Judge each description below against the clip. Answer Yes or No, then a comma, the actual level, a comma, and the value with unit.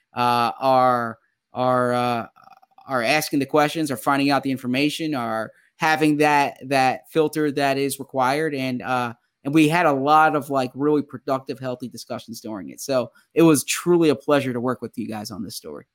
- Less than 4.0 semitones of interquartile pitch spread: Yes, average, 3.2 semitones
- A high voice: No, low, 135 Hz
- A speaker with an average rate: Yes, average, 190 wpm